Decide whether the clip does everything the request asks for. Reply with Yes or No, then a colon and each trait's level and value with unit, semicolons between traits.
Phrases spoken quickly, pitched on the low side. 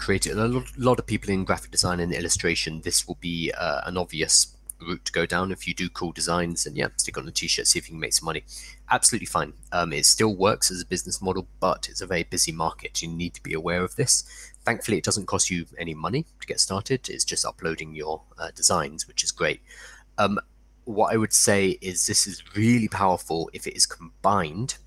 Yes: fast, 230 wpm; very low, 90 Hz